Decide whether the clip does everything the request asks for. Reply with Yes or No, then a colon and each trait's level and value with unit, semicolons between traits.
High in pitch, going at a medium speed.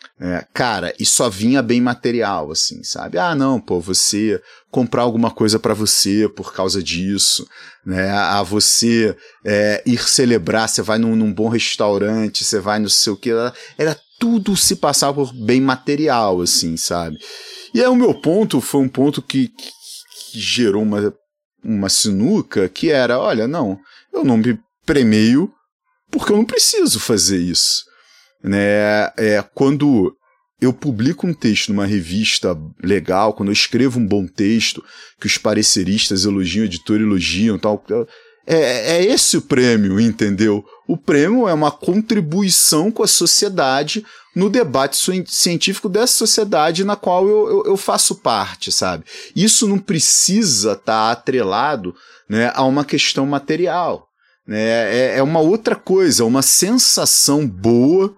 No: low, 125 Hz; average, 150 wpm